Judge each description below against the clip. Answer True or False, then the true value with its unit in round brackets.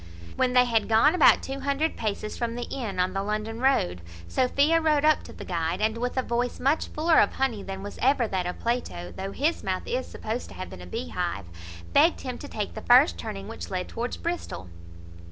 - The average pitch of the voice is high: True (230 Hz)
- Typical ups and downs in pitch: False (6.4 semitones)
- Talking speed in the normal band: False (225 wpm)